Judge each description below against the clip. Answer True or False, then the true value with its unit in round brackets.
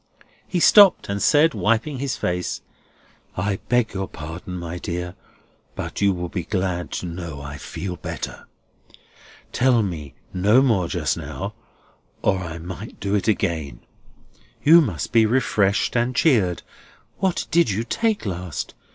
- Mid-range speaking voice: False (95 Hz)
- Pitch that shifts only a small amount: False (5.6 semitones)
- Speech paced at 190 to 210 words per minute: False (145 wpm)